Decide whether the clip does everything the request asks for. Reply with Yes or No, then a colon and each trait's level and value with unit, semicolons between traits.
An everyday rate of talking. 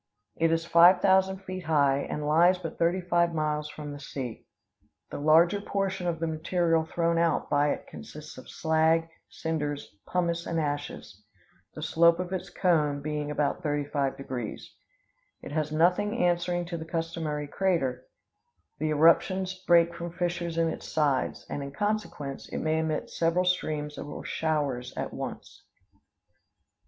Yes: average, 155 wpm